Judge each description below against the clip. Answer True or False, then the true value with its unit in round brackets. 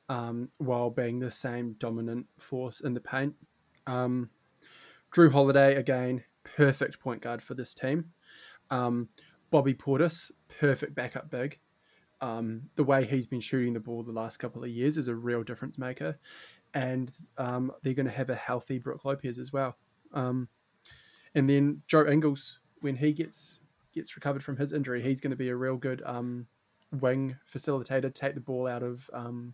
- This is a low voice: True (130 Hz)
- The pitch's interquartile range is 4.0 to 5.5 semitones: False (2.4 semitones)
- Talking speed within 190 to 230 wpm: False (175 wpm)